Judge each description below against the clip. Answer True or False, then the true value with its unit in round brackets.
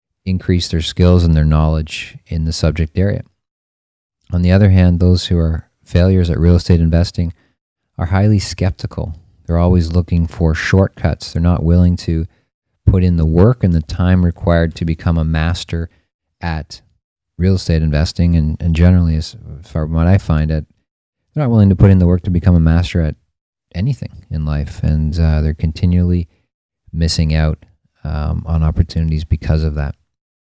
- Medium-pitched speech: False (85 Hz)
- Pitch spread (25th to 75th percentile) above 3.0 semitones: False (2.4 semitones)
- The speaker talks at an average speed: True (175 wpm)